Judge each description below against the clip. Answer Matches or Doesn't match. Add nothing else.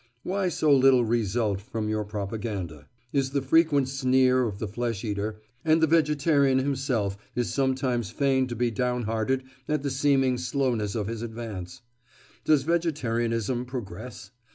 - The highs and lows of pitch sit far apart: Doesn't match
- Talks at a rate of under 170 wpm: Matches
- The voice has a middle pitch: Doesn't match